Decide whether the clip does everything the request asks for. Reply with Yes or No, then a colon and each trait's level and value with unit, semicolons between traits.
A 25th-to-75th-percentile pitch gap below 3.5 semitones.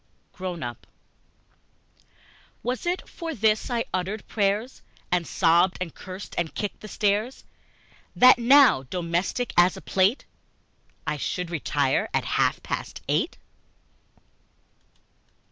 No: average, 5.2 semitones